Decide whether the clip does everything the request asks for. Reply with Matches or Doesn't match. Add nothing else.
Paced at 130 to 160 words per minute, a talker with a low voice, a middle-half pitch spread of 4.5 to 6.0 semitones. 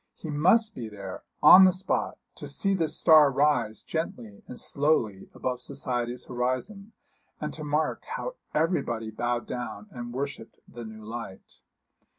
Matches